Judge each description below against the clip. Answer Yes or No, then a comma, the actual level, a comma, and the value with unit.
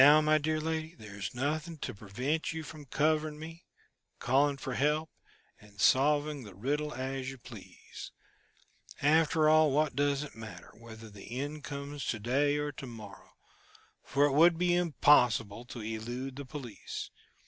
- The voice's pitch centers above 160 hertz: No, medium, 145 Hz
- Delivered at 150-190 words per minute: Yes, average, 160 wpm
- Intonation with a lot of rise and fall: No, average, 4.0 semitones